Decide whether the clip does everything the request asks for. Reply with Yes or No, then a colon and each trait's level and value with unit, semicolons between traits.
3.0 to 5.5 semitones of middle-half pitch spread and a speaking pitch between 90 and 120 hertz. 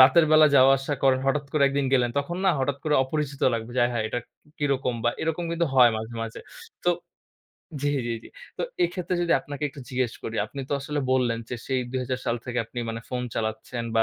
No: average, 3.3 semitones; low, 130 Hz